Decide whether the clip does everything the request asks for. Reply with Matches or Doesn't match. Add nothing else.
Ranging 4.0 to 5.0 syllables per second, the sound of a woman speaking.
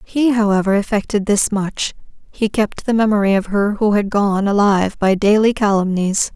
Matches